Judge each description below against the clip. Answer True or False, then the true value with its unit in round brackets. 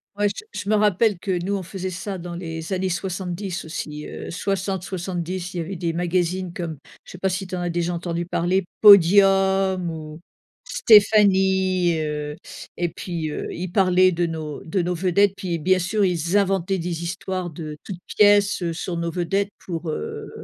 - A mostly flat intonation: True (2.3 semitones)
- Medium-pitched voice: True (180 Hz)